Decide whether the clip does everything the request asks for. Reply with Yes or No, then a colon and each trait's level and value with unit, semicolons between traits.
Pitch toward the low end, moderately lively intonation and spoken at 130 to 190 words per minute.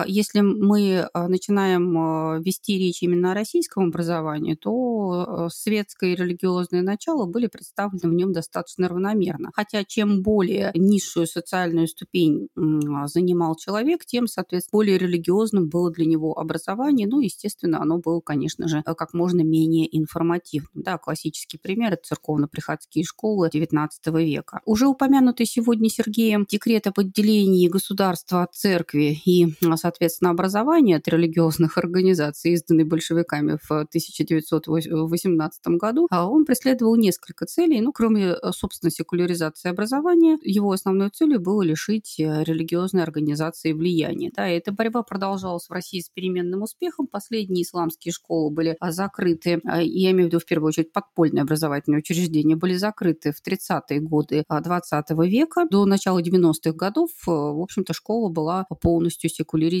No: medium, 175 Hz; average, 3.7 semitones; average, 135 wpm